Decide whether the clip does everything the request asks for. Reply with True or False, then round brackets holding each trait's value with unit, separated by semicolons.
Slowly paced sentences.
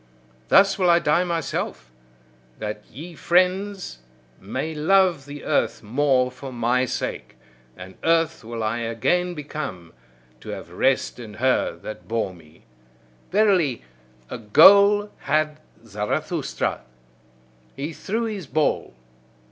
True (120 wpm)